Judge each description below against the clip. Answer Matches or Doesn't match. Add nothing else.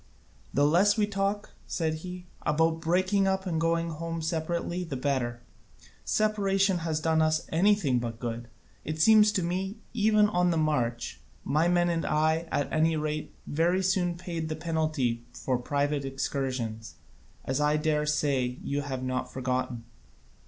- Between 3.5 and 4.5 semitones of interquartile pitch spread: Matches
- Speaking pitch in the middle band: Matches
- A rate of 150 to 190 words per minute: Matches